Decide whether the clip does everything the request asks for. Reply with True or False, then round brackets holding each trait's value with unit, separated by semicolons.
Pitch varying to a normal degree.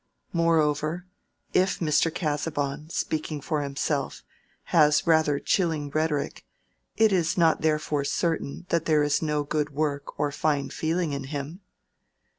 False (2.0 semitones)